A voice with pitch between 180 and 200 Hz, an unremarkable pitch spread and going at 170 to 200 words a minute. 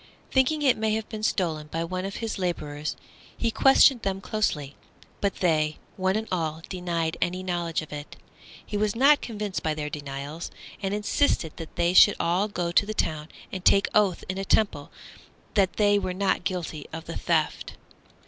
Yes: medium, 185 Hz; average, 4.4 semitones; average, 185 wpm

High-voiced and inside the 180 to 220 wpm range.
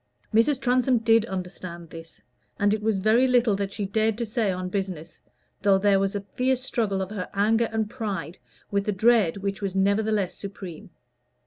Yes: high, 205 Hz; average, 185 wpm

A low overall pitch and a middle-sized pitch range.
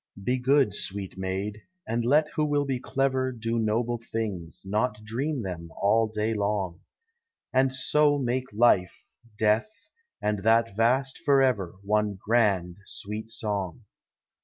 Yes: low, 115 Hz; average, 4.1 semitones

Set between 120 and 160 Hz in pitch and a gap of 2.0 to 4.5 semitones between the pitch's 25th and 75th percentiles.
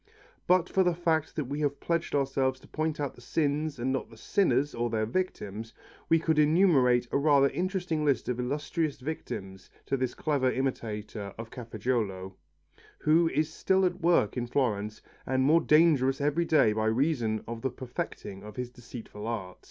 No: low, 135 Hz; average, 5.3 semitones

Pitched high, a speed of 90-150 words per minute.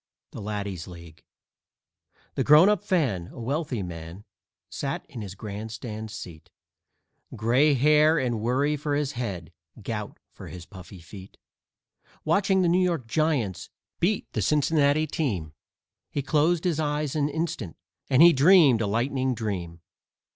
No: low, 130 Hz; average, 145 wpm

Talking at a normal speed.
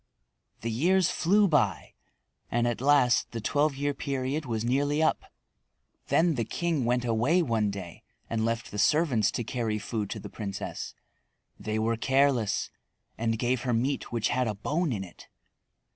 Yes: average, 165 wpm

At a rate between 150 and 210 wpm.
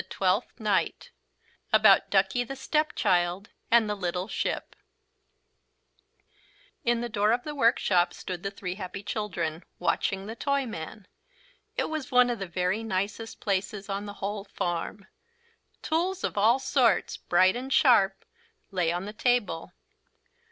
No: slow, 135 wpm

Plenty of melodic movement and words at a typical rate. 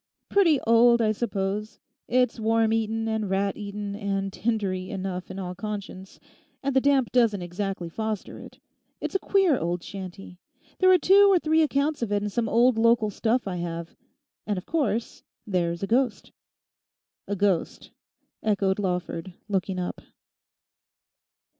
No: average, 3.8 semitones; average, 155 wpm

